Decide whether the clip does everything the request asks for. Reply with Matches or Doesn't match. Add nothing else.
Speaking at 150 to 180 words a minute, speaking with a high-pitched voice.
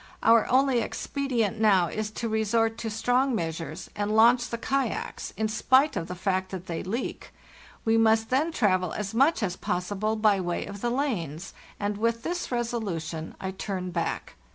Matches